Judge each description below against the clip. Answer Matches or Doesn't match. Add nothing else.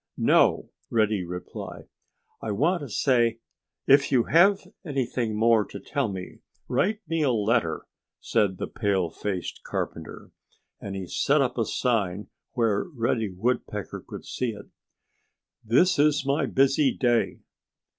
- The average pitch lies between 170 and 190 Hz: Doesn't match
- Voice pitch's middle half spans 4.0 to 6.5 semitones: Matches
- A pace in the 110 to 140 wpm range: Matches